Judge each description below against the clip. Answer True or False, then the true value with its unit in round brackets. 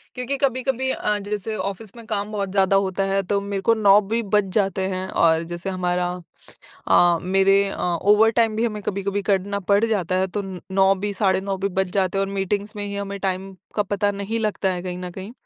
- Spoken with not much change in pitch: True (1.7 semitones)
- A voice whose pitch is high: True (200 Hz)